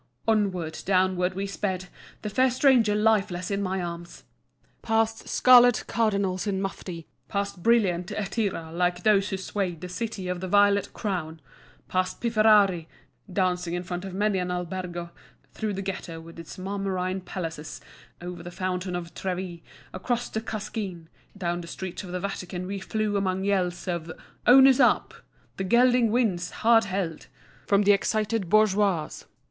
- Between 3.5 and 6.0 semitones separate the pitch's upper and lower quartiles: No, average, 2.9 semitones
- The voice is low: No, high, 190 Hz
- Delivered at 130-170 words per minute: Yes, average, 155 wpm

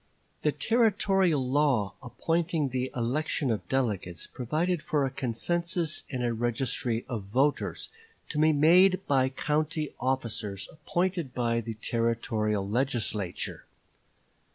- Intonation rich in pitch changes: No, average, 5.0 semitones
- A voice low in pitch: Yes, low, 130 Hz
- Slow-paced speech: Yes, slow, 115 wpm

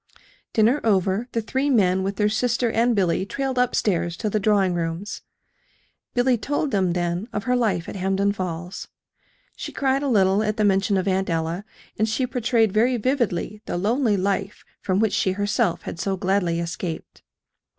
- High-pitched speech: Yes, high, 205 Hz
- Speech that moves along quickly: No, average, 180 wpm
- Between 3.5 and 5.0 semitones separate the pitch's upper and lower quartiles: Yes, average, 3.8 semitones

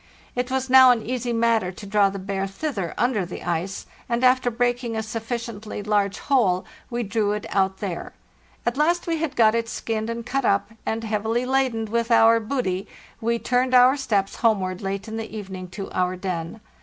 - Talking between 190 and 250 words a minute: Yes, average, 195 wpm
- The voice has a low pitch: No, high, 225 Hz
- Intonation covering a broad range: No, average, 3.7 semitones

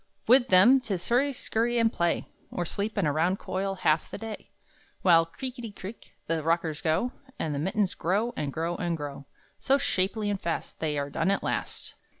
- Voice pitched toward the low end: No, medium, 185 Hz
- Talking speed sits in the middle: Yes, average, 190 wpm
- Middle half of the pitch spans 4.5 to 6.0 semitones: Yes, wide, 5.5 semitones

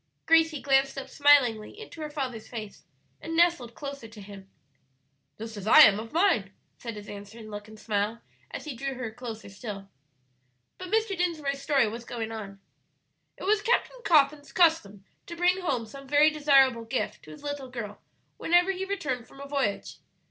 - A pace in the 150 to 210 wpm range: Yes, average, 175 wpm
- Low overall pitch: No, very high, 265 Hz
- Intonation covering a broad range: Yes, wide, 6.1 semitones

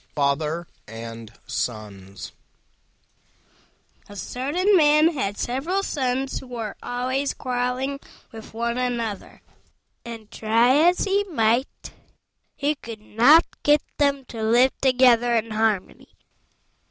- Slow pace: Yes, slow, 110 wpm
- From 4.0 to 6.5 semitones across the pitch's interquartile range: Yes, average, 4.3 semitones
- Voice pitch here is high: Yes, high, 245 Hz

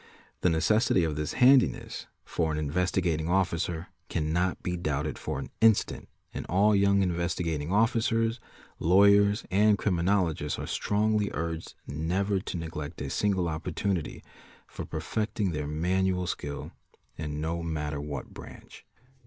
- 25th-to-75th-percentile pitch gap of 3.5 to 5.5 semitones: Yes, average, 4.3 semitones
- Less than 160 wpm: Yes, average, 140 wpm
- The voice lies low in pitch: Yes, very low, 90 Hz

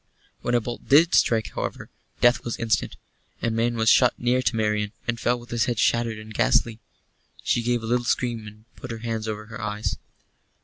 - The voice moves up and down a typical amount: No, narrow, 1.7 semitones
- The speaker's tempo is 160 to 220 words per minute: Yes, fast, 205 wpm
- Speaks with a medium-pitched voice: No, low, 115 Hz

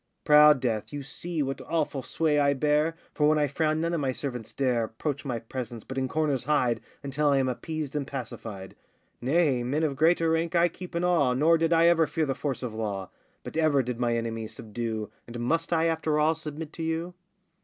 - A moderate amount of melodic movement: Yes, average, 4.5 semitones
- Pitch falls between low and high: Yes, medium, 145 Hz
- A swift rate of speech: Yes, fast, 215 wpm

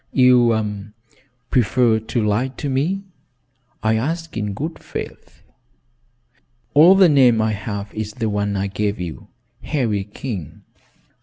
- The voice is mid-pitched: No, low, 110 Hz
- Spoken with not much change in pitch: No, average, 4.3 semitones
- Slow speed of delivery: Yes, slow, 130 wpm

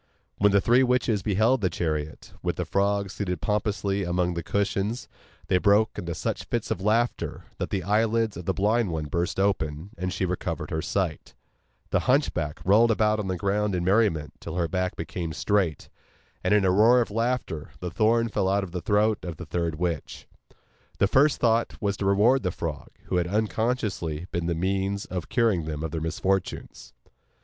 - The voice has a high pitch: No, very low, 95 Hz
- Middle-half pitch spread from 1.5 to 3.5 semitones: No, average, 3.9 semitones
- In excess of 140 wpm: Yes, average, 190 wpm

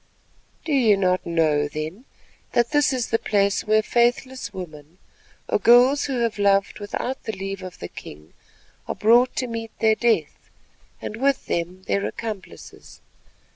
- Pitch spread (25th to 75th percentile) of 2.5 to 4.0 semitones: No, average, 4.5 semitones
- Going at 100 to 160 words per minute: Yes, average, 155 wpm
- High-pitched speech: Yes, high, 215 Hz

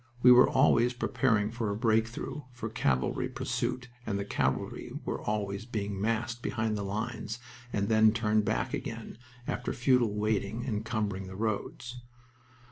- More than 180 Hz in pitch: No, low, 110 Hz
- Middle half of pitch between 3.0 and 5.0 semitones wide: No, narrow, 2.4 semitones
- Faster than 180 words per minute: No, average, 150 wpm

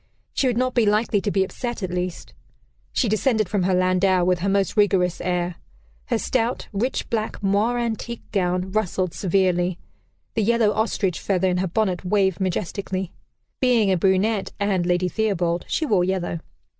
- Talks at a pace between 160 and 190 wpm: Yes, average, 170 wpm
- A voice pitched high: Yes, high, 195 Hz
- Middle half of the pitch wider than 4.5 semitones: No, average, 3.2 semitones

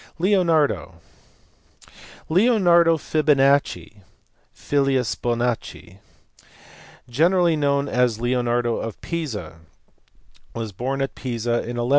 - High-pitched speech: No, low, 135 Hz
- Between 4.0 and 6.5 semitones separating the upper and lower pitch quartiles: Yes, average, 5.1 semitones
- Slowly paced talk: Yes, slow, 95 wpm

